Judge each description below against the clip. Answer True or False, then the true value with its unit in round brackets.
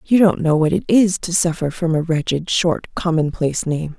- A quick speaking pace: True (210 wpm)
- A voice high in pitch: False (165 Hz)